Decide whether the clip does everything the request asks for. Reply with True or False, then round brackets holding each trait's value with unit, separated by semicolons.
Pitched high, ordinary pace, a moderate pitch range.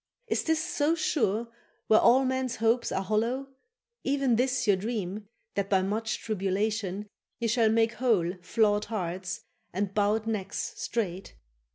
True (220 Hz; 145 wpm; 3.4 semitones)